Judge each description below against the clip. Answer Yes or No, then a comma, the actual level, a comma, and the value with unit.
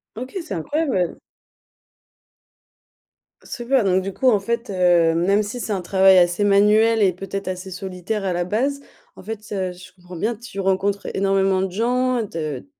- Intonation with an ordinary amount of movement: Yes, average, 3.4 semitones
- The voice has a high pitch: Yes, high, 195 Hz